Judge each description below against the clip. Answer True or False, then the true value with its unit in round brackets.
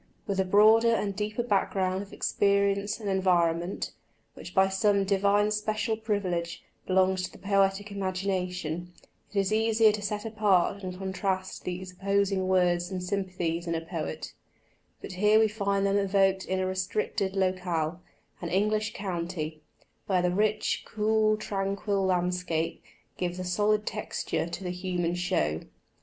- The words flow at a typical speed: True (150 wpm)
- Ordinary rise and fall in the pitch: False (2.2 semitones)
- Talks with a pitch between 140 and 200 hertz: True (190 Hz)